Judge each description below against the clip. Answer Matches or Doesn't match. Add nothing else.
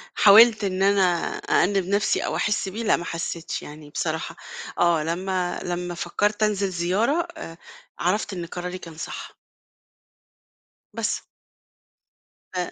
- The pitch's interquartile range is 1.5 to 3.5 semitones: Matches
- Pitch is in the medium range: Matches